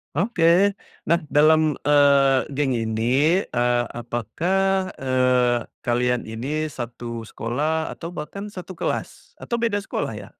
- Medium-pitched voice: Yes, medium, 145 Hz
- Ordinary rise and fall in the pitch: No, wide, 6.0 semitones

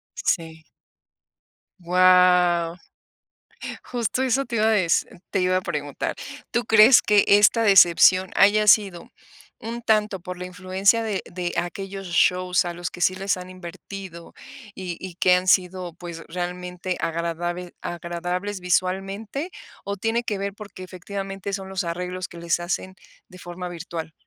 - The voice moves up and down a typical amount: No, narrow, 2.3 semitones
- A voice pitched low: No, medium, 185 Hz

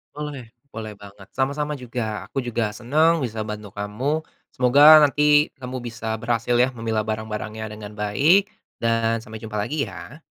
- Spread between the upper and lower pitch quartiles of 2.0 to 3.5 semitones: No, average, 4.6 semitones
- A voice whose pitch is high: No, low, 115 Hz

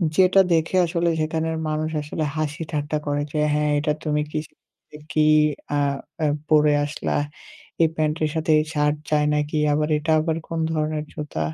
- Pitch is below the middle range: No, medium, 155 Hz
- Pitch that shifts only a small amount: Yes, narrow, 1.2 semitones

